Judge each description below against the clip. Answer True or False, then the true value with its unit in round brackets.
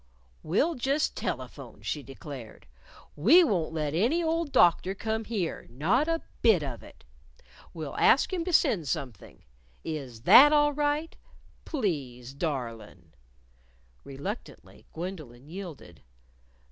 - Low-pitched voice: False (175 Hz)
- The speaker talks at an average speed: False (120 wpm)